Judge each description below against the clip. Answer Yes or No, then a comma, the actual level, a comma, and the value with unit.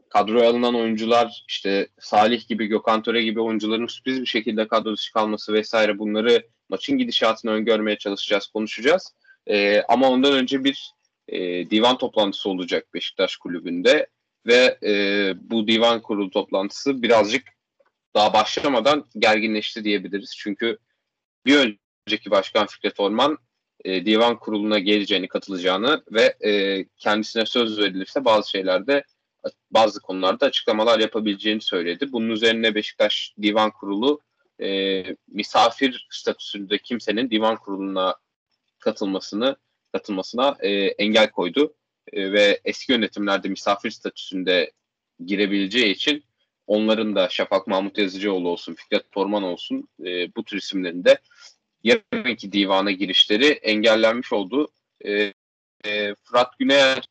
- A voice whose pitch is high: No, low, 110 Hz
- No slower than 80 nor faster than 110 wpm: No, average, 120 wpm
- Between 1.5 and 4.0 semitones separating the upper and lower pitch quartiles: Yes, average, 2.7 semitones